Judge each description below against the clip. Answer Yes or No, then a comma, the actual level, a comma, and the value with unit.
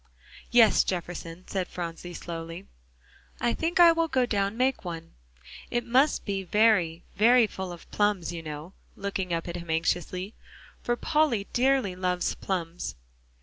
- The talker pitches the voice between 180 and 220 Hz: Yes, high, 190 Hz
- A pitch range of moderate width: No, wide, 5.7 semitones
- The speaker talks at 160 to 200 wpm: No, average, 145 wpm